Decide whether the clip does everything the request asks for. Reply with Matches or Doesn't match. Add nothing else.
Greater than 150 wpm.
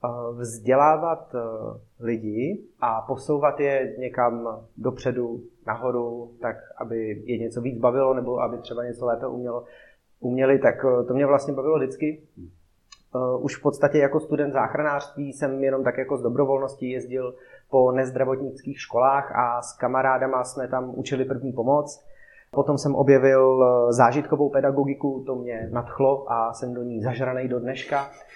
Doesn't match